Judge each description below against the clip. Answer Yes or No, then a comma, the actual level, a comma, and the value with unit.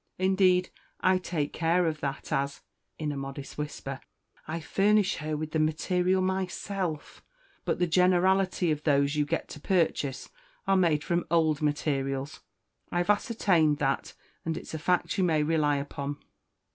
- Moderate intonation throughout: Yes, average, 3.8 semitones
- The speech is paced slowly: No, average, 155 wpm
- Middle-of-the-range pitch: Yes, medium, 160 Hz